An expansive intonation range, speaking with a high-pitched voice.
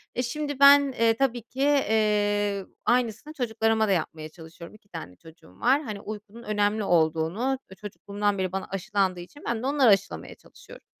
No: average, 4.6 semitones; high, 210 Hz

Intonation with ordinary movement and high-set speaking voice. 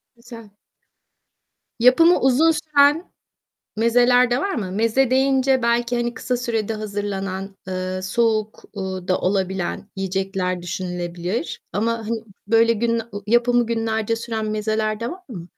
Yes: average, 3.9 semitones; high, 225 Hz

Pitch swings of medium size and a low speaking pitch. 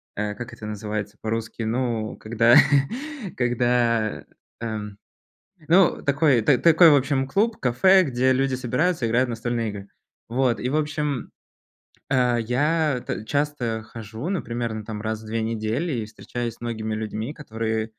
Yes: average, 3.6 semitones; low, 120 Hz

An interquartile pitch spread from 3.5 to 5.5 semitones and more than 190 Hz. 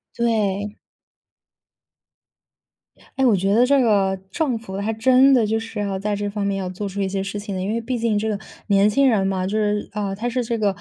No: average, 2.7 semitones; high, 210 Hz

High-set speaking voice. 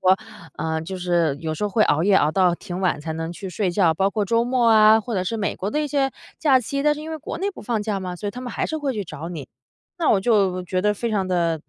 Yes: high, 195 Hz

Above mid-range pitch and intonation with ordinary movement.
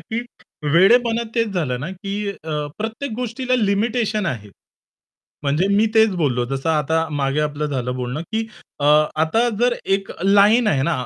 No: high, 195 Hz; wide, 6.9 semitones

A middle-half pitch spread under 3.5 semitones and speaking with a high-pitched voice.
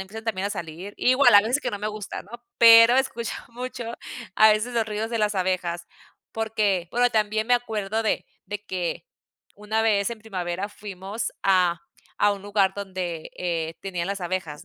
Yes: average, 3.0 semitones; high, 205 Hz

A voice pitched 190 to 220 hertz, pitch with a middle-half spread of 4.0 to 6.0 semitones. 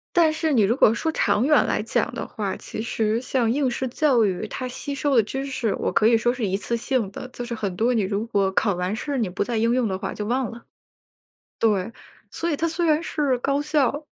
No: high, 235 Hz; average, 4.4 semitones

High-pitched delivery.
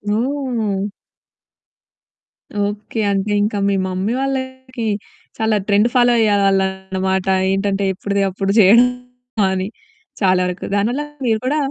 Yes: high, 205 Hz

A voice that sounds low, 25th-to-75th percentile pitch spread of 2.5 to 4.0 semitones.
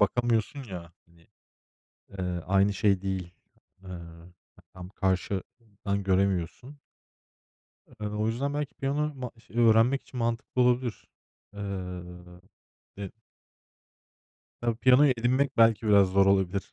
No: low, 100 Hz; average, 4.6 semitones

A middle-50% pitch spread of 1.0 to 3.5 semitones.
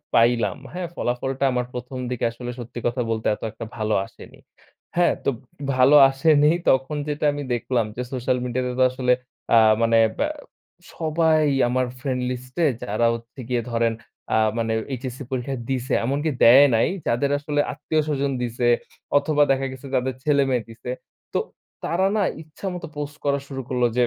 Yes: average, 3.1 semitones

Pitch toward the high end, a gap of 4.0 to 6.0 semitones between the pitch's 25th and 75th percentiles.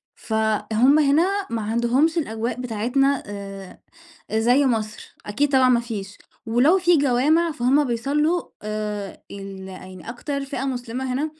Yes: high, 245 Hz; average, 4.6 semitones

